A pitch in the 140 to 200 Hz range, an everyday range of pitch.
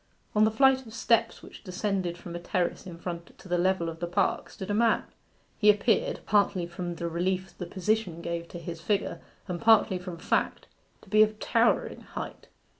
Yes: medium, 185 Hz; average, 3.6 semitones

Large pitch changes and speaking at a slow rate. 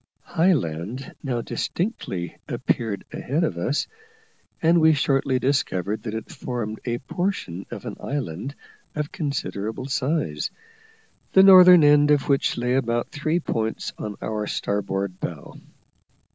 Yes: wide, 6.1 semitones; slow, 130 wpm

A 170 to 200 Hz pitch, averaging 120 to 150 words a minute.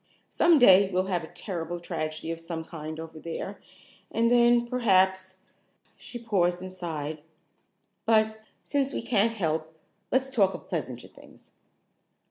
Yes: medium, 185 Hz; average, 145 wpm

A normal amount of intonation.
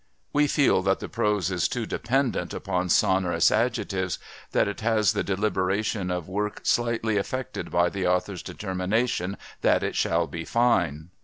Yes: average, 3.7 semitones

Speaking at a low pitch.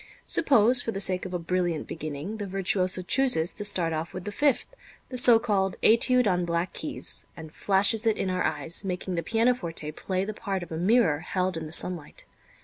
No: medium, 185 Hz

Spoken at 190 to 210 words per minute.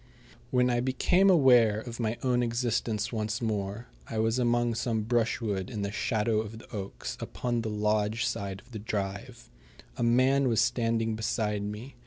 No: average, 170 wpm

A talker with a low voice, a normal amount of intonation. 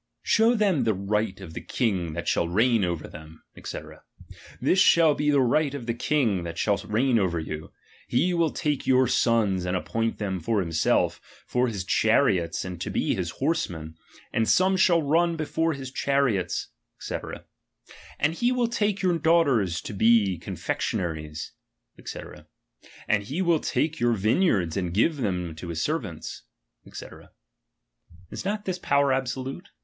No: low, 115 Hz; wide, 9.0 semitones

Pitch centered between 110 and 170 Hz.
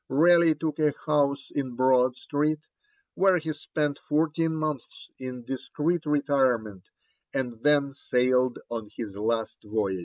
Yes: medium, 140 Hz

